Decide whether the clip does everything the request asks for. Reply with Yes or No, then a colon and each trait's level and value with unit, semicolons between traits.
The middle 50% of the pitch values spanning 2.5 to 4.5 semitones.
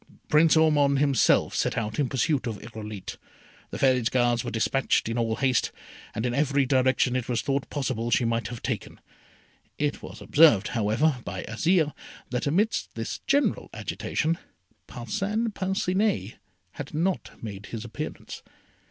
No: average, 4.9 semitones